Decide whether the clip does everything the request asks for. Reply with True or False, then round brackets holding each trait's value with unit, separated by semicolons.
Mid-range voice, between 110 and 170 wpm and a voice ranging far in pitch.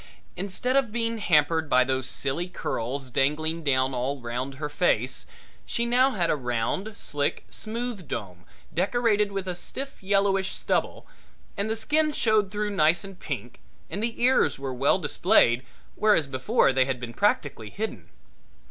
True (175 Hz; 155 wpm; 8.3 semitones)